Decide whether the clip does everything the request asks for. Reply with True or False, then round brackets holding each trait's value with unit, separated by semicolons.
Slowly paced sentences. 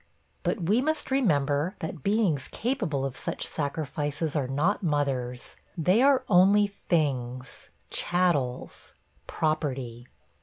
True (110 wpm)